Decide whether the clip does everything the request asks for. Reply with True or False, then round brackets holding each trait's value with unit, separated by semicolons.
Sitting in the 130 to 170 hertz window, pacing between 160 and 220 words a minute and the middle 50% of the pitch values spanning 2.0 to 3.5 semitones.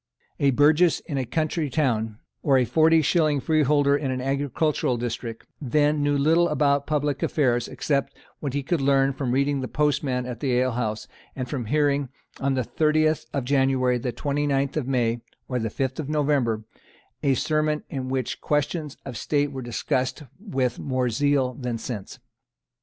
True (140 Hz; 170 wpm; 2.7 semitones)